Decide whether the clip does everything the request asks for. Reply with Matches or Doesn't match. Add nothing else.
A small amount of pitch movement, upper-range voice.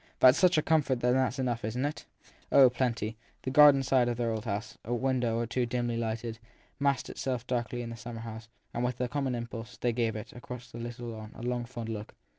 Doesn't match